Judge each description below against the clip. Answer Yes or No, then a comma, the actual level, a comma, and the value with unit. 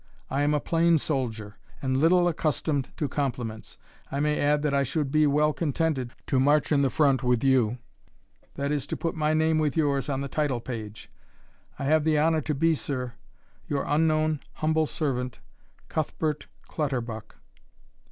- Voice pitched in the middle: Yes, medium, 145 Hz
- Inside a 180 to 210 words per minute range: No, average, 170 wpm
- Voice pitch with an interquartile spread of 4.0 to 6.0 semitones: No, average, 2.9 semitones